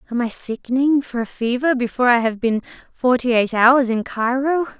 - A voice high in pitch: Yes, high, 245 Hz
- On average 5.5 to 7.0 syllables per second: No, 5.3 syllables/s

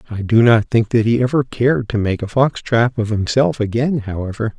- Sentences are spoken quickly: Yes, fast, 225 wpm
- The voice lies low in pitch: Yes, low, 115 Hz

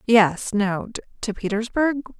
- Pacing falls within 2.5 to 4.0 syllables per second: Yes, 3.5 syllables/s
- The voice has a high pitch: Yes, high, 220 Hz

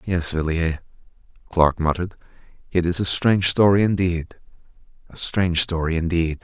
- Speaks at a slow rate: Yes, slow, 130 wpm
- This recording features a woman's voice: No, male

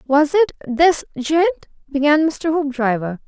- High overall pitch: Yes, very high, 295 Hz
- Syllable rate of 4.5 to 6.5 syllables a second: No, 4.0 syllables/s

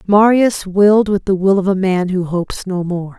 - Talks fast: Yes, fast, 225 wpm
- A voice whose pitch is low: No, high, 190 Hz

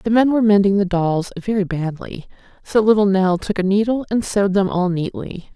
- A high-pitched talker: Yes, high, 195 Hz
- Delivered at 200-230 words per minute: Yes, fast, 205 wpm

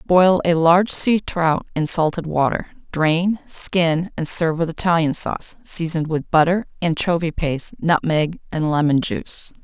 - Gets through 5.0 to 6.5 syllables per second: No, 4.6 syllables/s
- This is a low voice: No, medium, 165 Hz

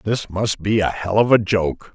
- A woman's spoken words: No, male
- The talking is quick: Yes, fast, 245 wpm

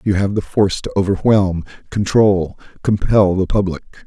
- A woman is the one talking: No, male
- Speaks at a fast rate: No, average, 150 wpm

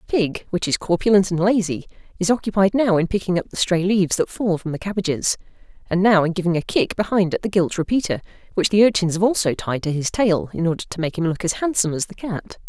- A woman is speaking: Yes, female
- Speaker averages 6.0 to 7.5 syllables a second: Yes, 6.3 syllables/s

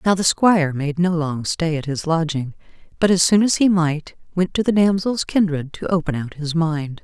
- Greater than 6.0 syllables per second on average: No, 4.9 syllables/s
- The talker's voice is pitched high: No, medium, 170 Hz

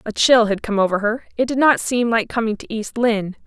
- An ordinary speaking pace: No, fast, 260 wpm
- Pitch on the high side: Yes, high, 225 Hz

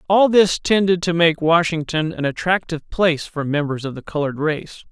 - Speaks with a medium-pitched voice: Yes, medium, 165 Hz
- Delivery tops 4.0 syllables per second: Yes, 5.5 syllables/s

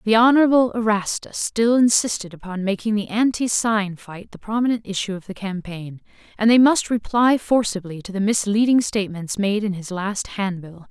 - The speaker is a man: No, female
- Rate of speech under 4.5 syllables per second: No, 5.1 syllables/s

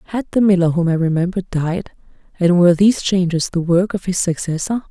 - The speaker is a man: No, female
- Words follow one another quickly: No, average, 195 wpm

